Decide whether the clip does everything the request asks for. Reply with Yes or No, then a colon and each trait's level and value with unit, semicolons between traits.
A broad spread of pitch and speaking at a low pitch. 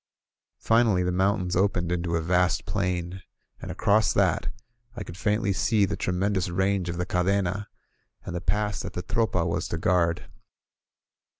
No: narrow, 2.4 semitones; very low, 90 Hz